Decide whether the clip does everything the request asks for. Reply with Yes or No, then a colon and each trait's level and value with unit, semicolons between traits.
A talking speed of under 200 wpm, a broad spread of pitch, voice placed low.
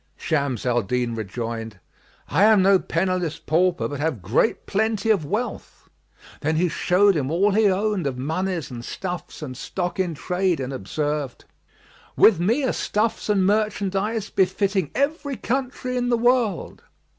No: average, 155 wpm; wide, 6.3 semitones; medium, 185 Hz